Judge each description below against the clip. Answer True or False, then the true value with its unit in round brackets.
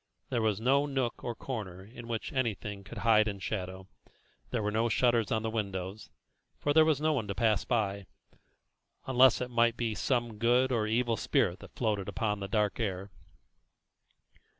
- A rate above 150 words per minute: True (175 wpm)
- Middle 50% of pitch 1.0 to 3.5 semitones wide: True (2.9 semitones)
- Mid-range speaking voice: False (110 Hz)